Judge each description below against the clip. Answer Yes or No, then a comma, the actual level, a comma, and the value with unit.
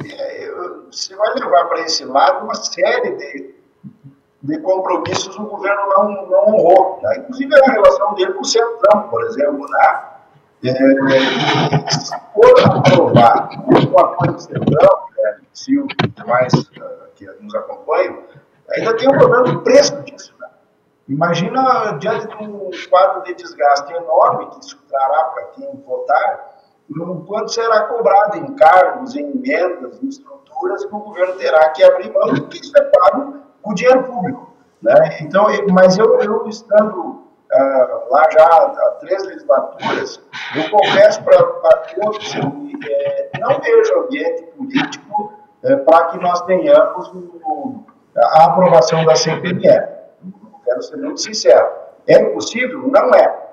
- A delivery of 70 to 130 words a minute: No, average, 150 wpm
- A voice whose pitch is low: No, high, 220 Hz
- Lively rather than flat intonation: Yes, wide, 8.4 semitones